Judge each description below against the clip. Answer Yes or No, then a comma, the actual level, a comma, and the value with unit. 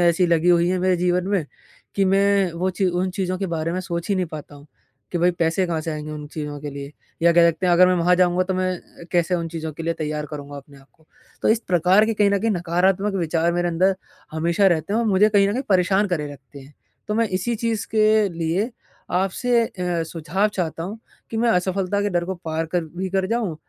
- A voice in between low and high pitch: Yes, medium, 180 Hz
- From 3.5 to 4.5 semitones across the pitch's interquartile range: No, average, 3.0 semitones